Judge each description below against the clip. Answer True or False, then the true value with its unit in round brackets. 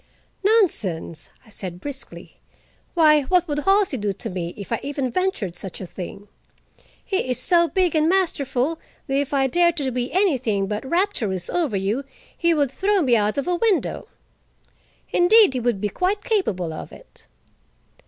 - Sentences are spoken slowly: False (170 wpm)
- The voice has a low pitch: False (275 Hz)